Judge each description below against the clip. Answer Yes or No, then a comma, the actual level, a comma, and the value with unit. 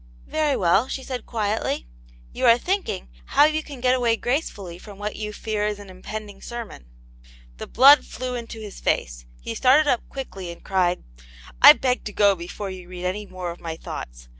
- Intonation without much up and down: No, wide, 5.5 semitones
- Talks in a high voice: Yes, high, 210 Hz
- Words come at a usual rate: Yes, average, 195 wpm